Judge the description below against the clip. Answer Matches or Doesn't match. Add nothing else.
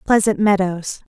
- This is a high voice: Matches